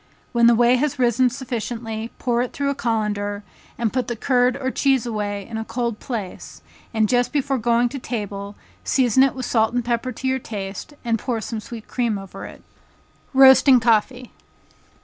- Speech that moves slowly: No, average, 185 wpm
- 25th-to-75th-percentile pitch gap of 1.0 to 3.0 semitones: Yes, narrow, 2.6 semitones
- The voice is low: No, high, 235 Hz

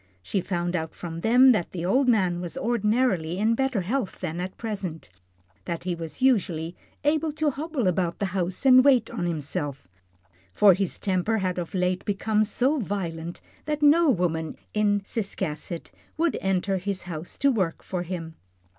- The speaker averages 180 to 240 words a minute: No, average, 170 wpm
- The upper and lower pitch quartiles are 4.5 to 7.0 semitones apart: Yes, average, 5.2 semitones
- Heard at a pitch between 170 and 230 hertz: Yes, high, 190 Hz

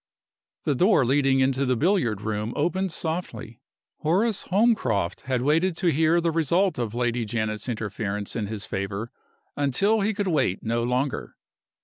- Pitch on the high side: No, low, 135 Hz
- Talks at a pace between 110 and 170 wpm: Yes, average, 150 wpm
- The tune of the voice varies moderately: No, wide, 7.3 semitones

